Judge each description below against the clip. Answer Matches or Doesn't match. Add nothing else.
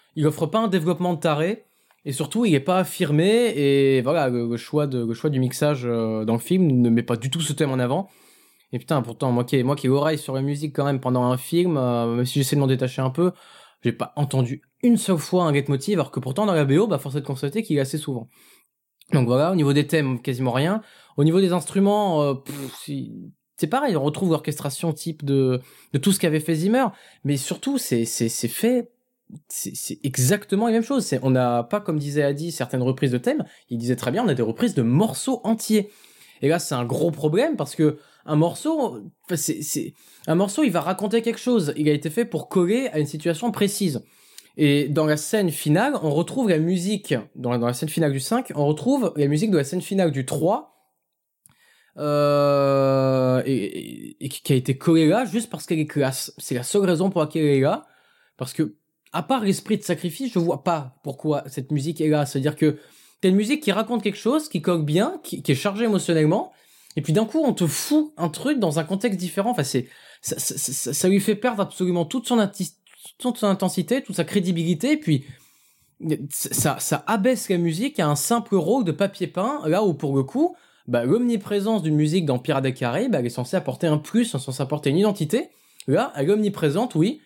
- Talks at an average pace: Doesn't match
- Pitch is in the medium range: Matches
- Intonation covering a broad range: Matches